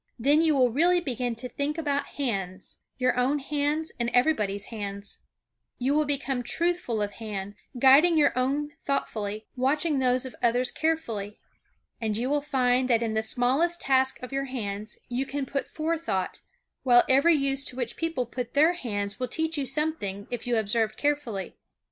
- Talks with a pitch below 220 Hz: No, very high, 255 Hz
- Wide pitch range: No, average, 4.3 semitones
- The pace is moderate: Yes, average, 170 wpm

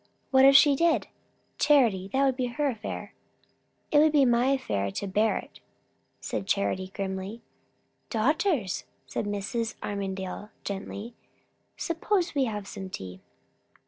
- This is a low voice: No, high, 225 Hz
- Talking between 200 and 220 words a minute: No, slow, 135 wpm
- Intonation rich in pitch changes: Yes, wide, 5.8 semitones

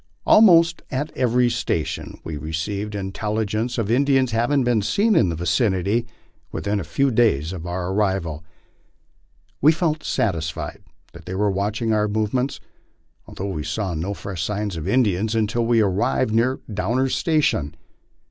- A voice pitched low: Yes, low, 105 Hz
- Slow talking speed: No, average, 150 wpm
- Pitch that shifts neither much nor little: Yes, average, 4.7 semitones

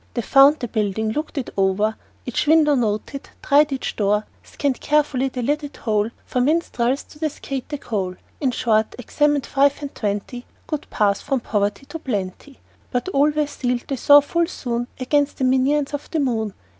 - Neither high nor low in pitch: No, very high, 265 Hz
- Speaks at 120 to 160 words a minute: No, average, 180 wpm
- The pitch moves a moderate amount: Yes, average, 4.8 semitones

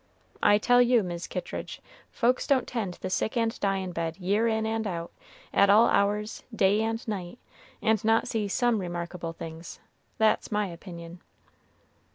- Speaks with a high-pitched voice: Yes, high, 205 Hz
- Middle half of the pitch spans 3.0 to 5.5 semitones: Yes, average, 4.0 semitones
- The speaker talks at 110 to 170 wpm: Yes, average, 160 wpm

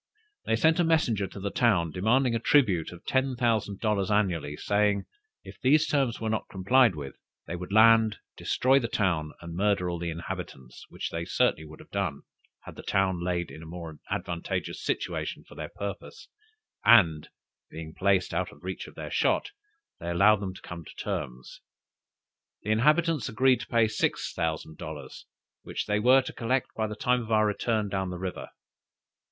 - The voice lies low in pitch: Yes, low, 100 Hz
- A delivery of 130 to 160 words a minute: No, average, 185 wpm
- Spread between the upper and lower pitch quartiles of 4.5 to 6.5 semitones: Yes, average, 5.0 semitones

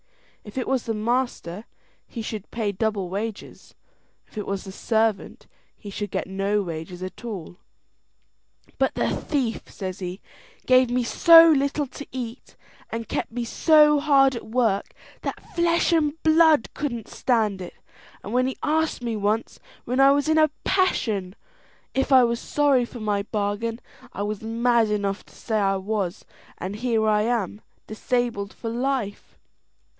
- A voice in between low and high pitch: No, high, 230 Hz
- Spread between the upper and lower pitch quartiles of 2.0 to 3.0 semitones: No, average, 4.4 semitones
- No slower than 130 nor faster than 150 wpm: No, average, 165 wpm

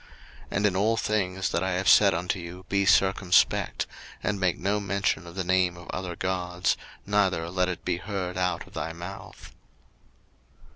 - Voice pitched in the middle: No, very low, 95 Hz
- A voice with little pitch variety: Yes, narrow, 1.7 semitones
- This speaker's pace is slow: No, average, 180 wpm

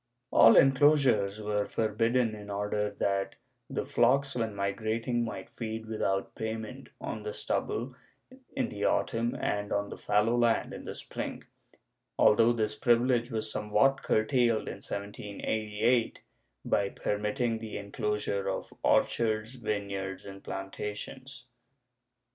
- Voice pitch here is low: Yes, low, 110 Hz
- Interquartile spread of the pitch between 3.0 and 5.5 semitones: No, narrow, 2.4 semitones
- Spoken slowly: Yes, slow, 125 wpm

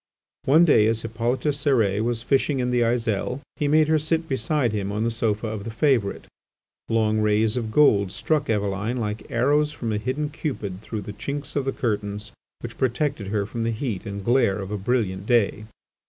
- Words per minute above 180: Yes, average, 195 wpm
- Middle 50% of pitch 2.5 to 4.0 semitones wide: No, average, 4.4 semitones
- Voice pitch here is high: No, low, 115 Hz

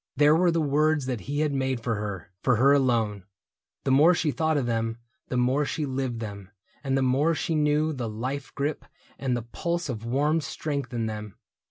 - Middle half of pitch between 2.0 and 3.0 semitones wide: No, average, 4.3 semitones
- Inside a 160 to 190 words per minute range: No, fast, 205 wpm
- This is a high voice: No, low, 135 Hz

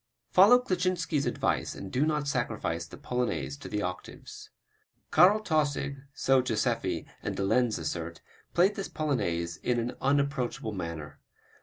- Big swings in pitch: Yes, wide, 9.0 semitones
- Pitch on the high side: No, low, 125 Hz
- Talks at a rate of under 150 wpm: Yes, average, 140 wpm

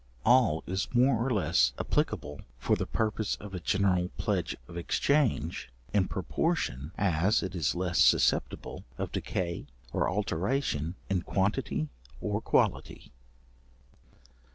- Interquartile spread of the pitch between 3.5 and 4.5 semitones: Yes, average, 4.1 semitones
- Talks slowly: Yes, slow, 125 wpm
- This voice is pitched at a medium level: No, very low, 95 Hz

